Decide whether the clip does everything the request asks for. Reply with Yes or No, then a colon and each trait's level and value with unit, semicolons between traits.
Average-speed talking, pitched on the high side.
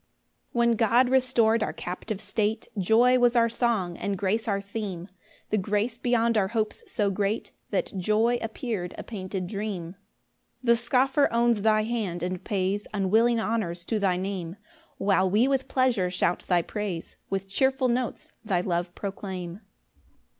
Yes: average, 160 wpm; high, 210 Hz